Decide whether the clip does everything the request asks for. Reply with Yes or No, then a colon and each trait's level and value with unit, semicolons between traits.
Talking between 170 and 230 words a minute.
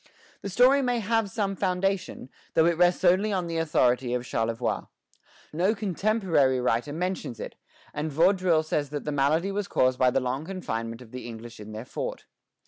Yes: average, 180 wpm